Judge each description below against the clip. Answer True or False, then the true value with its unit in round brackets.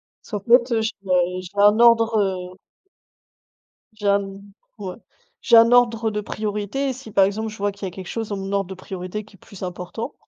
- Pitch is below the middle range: False (210 Hz)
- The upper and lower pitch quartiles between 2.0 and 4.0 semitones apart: True (2.7 semitones)